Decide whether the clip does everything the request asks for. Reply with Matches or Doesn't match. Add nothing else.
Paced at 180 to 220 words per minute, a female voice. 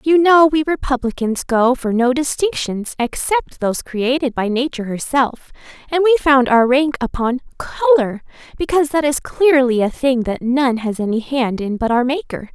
Doesn't match